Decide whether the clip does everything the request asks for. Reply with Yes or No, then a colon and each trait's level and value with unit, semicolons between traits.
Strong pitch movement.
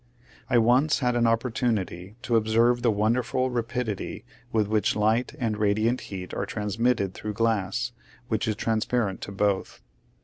No: narrow, 2.6 semitones